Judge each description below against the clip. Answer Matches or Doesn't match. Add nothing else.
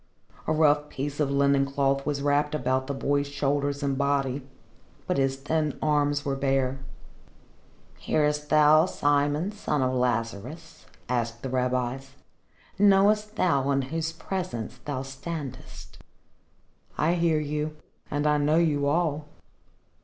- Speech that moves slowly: Matches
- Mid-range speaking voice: Matches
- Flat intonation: Matches